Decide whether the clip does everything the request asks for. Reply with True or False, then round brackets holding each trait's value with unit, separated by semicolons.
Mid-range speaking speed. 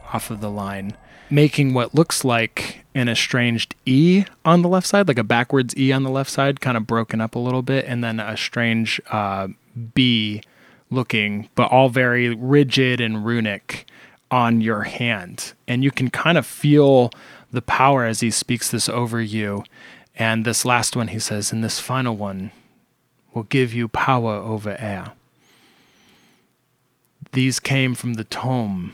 True (170 wpm)